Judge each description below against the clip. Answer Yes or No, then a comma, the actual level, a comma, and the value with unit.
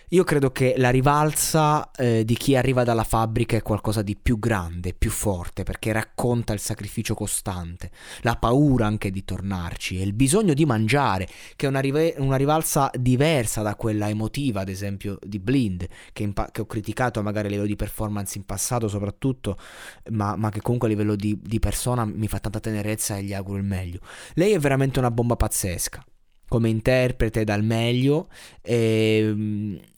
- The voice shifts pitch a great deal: No, average, 3.6 semitones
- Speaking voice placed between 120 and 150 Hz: No, low, 110 Hz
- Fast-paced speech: Yes, fast, 180 wpm